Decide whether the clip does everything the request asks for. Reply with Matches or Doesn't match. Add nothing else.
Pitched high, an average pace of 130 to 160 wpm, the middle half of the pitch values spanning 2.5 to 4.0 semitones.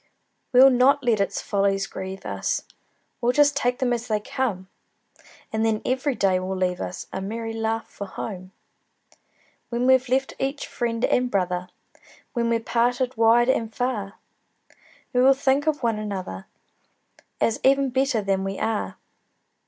Doesn't match